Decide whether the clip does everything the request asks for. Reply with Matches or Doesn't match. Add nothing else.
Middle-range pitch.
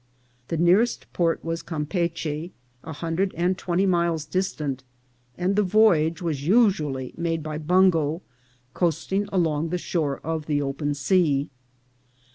Matches